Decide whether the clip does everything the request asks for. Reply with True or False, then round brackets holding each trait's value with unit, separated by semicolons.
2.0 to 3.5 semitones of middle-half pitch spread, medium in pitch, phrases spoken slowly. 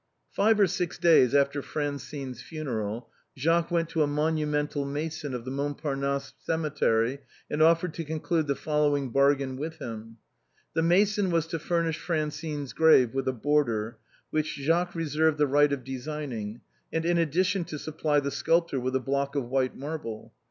False (3.1 semitones; 150 Hz; 165 wpm)